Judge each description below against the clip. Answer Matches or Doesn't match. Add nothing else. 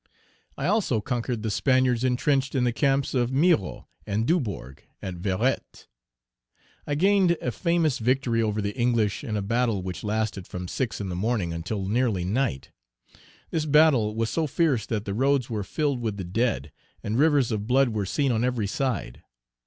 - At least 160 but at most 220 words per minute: Matches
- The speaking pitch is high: Doesn't match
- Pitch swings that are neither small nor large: Matches